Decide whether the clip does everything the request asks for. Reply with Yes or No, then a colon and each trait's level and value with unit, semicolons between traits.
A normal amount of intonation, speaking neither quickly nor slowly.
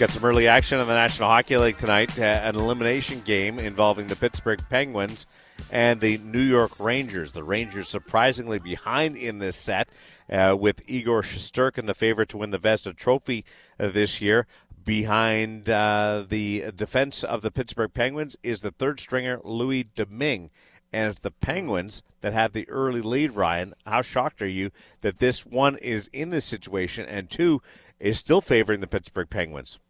Yes: average, 3.0 semitones; average, 170 wpm